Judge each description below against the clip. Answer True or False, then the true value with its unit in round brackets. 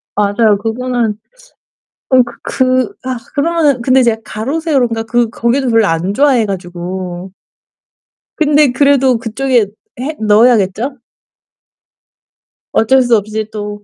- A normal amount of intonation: True (3.9 semitones)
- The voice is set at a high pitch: True (235 Hz)